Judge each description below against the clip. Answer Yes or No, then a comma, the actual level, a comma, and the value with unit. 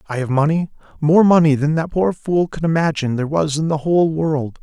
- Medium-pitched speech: Yes, medium, 155 Hz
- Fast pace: Yes, fast, 220 wpm